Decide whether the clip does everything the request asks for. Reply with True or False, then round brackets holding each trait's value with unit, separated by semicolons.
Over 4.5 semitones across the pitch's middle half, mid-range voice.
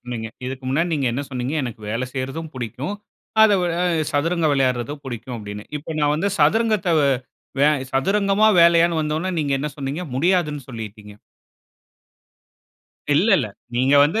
True (4.9 semitones; 145 Hz)